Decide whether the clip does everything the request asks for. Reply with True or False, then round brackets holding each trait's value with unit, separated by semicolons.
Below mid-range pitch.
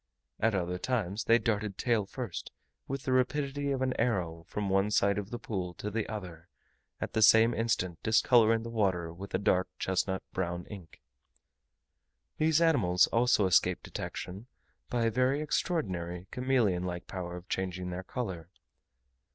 True (105 Hz)